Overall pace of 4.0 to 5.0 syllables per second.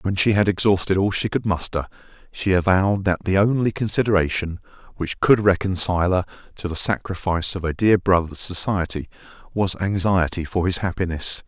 No: 5.5 syllables/s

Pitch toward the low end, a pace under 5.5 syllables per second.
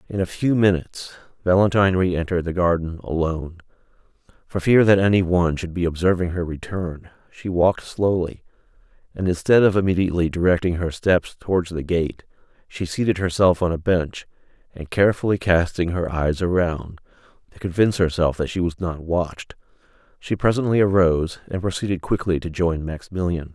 No: very low, 90 Hz; 5.7 syllables/s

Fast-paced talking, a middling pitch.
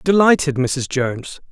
No: slow, 120 wpm; medium, 145 Hz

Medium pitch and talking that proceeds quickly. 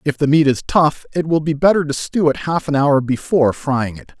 Yes: medium, 145 Hz; fast, 255 wpm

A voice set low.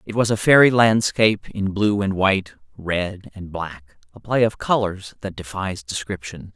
Yes: low, 100 Hz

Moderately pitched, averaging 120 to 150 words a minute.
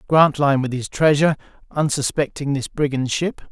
Yes: medium, 145 Hz; slow, 135 wpm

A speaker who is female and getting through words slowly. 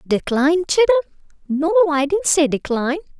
Yes: female; slow, 95 wpm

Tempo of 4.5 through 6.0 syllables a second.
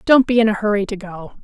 No: 6.4 syllables/s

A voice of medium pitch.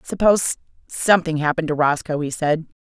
Yes: medium, 160 Hz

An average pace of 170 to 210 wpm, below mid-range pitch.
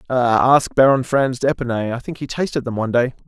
Yes: average, 200 wpm; low, 125 Hz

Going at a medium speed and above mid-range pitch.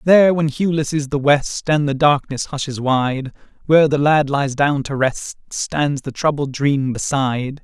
No: average, 180 wpm; medium, 140 Hz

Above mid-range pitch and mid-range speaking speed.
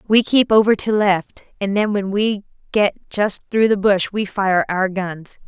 Yes: high, 200 Hz; average, 195 wpm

